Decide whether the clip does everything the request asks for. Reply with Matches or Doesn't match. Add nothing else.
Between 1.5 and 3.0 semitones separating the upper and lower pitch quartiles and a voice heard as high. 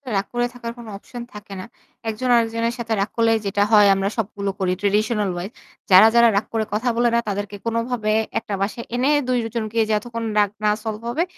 Matches